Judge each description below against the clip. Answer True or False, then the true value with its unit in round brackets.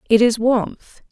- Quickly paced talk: False (160 wpm)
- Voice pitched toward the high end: True (230 Hz)